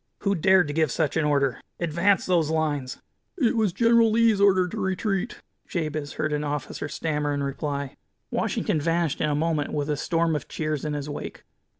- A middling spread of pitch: Yes, average, 4.3 semitones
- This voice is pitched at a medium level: Yes, medium, 155 Hz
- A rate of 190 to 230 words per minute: Yes, average, 195 wpm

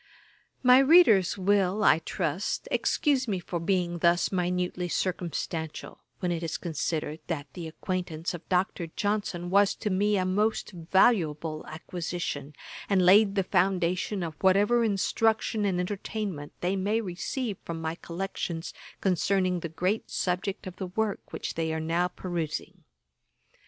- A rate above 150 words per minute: No, average, 140 wpm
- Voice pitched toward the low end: No, medium, 180 Hz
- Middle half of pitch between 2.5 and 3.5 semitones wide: Yes, average, 3.0 semitones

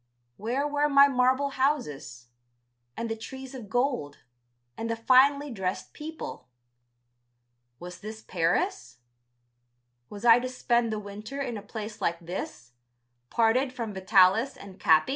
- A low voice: No, high, 230 Hz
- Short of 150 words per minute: Yes, slow, 135 wpm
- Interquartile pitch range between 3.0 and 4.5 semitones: No, average, 5.1 semitones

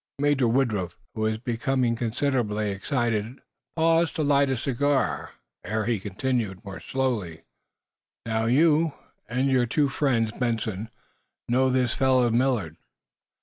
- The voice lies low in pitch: Yes, low, 120 Hz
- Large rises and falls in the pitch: No, average, 3.6 semitones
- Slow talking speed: Yes, slow, 125 wpm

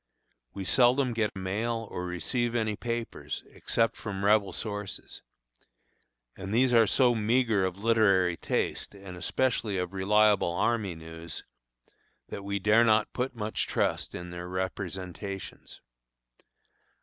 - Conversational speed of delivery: No, slow, 130 wpm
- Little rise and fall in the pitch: No, average, 3.5 semitones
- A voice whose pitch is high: No, low, 105 Hz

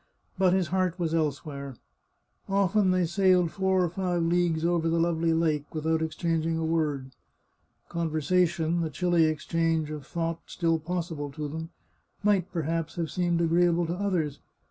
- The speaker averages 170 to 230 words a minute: No, average, 155 wpm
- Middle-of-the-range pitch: Yes, medium, 165 Hz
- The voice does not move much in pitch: Yes, narrow, 1.9 semitones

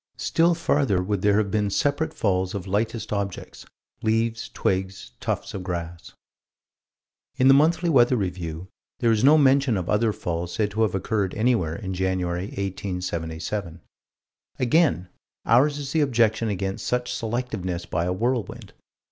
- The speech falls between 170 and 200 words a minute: No, average, 150 wpm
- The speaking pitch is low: Yes, low, 105 Hz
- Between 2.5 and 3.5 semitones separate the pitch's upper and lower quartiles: No, average, 4.8 semitones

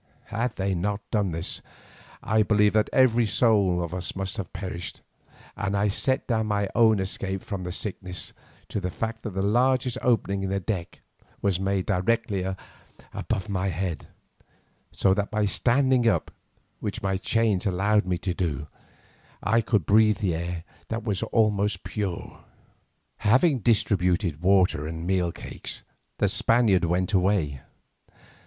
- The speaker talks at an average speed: Yes, average, 150 wpm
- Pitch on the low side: Yes, low, 100 Hz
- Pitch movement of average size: Yes, average, 3.2 semitones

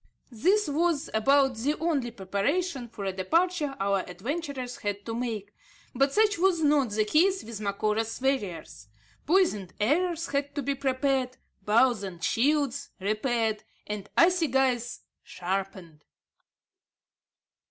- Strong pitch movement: Yes, wide, 6.0 semitones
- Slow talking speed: Yes, slow, 120 wpm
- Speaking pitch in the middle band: No, very high, 250 Hz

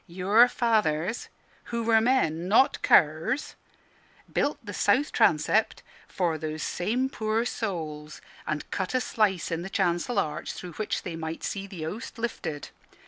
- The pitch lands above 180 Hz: Yes, high, 190 Hz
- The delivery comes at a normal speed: Yes, average, 145 wpm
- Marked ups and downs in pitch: Yes, wide, 6.1 semitones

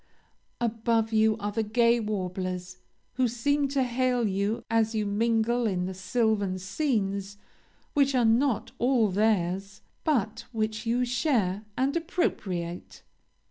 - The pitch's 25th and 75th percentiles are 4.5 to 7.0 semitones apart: No, average, 3.5 semitones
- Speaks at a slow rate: Yes, slow, 130 wpm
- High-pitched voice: Yes, high, 220 Hz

